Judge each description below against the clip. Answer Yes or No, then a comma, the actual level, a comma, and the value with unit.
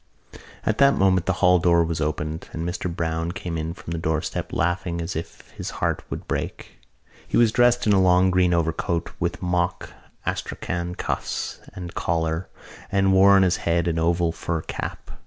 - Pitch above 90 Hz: No, very low, 85 Hz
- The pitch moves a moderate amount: No, narrow, 2.1 semitones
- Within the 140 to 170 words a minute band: No, average, 180 wpm